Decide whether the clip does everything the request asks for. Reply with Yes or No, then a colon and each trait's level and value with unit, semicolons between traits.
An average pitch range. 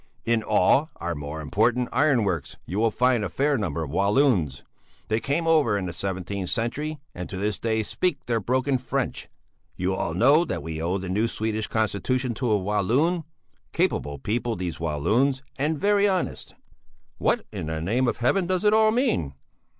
No: wide, 6.9 semitones